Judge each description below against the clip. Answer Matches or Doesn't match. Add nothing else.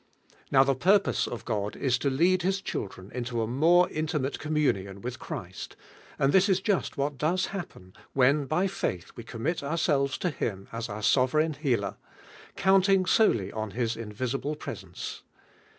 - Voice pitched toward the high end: Doesn't match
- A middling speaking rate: Matches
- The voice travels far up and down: Matches